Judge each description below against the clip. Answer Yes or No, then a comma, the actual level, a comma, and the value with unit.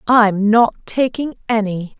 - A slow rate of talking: Yes, slow, 120 wpm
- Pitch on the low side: No, high, 220 Hz